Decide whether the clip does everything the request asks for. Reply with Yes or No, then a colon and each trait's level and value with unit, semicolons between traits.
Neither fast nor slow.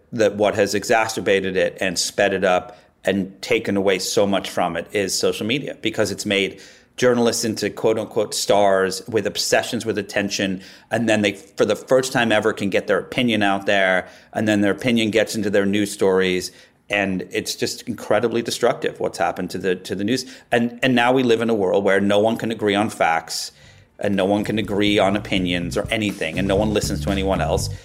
No: fast, 210 wpm